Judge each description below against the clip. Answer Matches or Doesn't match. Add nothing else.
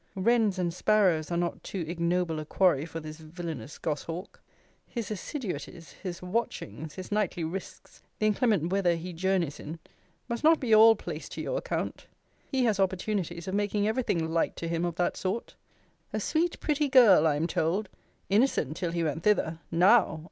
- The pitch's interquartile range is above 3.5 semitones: Matches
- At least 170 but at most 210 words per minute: Matches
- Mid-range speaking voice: Matches